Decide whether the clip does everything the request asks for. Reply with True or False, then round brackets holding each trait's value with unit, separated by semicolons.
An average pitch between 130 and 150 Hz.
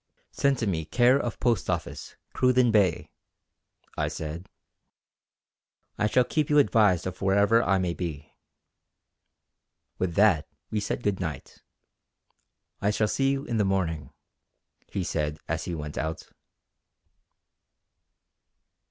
False (95 Hz)